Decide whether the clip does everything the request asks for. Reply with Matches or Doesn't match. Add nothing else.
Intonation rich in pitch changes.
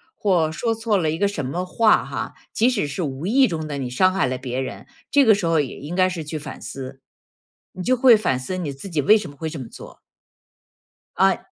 Matches